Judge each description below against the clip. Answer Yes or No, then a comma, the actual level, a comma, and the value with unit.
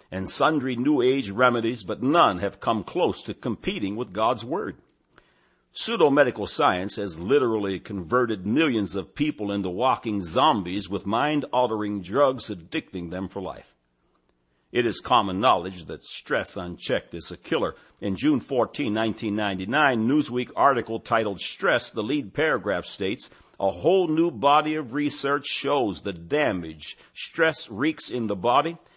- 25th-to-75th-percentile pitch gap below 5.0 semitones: No, wide, 5.4 semitones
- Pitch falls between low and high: No, low, 110 Hz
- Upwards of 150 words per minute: No, average, 145 wpm